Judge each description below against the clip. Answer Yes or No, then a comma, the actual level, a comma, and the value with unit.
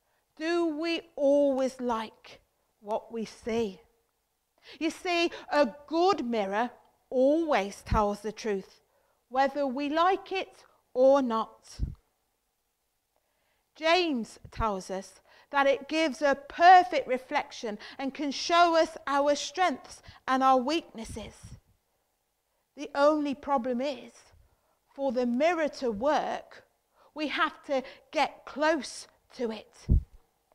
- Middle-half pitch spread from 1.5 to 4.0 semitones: No, average, 4.5 semitones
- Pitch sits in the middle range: No, very high, 280 Hz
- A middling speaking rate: No, slow, 110 wpm